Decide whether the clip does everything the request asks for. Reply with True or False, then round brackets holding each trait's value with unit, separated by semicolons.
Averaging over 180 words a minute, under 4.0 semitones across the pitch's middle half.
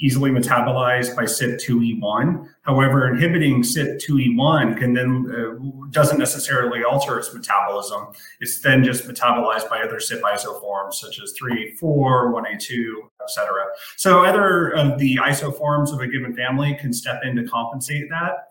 False (145 wpm; 3.2 semitones)